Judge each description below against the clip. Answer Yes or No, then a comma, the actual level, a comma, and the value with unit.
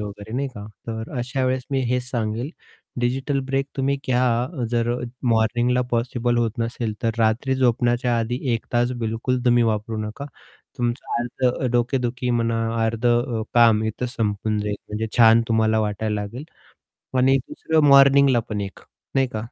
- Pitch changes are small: Yes, narrow, 2.2 semitones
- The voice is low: Yes, low, 120 Hz